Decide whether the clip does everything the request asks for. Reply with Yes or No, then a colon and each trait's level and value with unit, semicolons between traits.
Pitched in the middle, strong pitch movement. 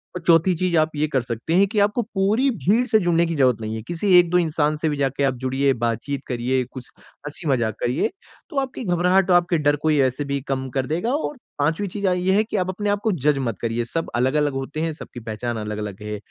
Yes: medium, 155 Hz; wide, 5.9 semitones